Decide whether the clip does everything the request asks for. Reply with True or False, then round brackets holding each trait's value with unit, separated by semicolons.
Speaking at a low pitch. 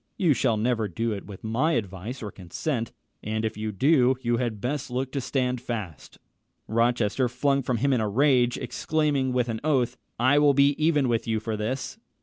True (125 Hz)